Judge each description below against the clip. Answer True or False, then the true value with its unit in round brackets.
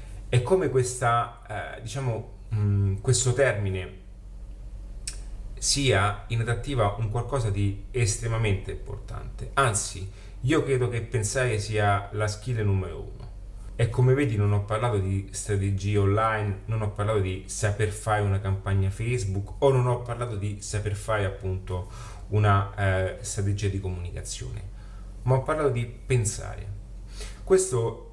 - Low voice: True (105 Hz)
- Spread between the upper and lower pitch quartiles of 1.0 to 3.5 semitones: True (3.0 semitones)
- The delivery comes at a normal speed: True (135 wpm)